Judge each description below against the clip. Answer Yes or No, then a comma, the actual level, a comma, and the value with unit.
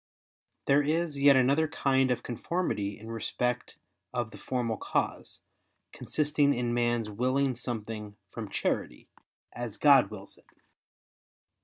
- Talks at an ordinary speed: No, slow, 125 wpm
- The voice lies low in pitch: Yes, low, 125 Hz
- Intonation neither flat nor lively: Yes, average, 3.7 semitones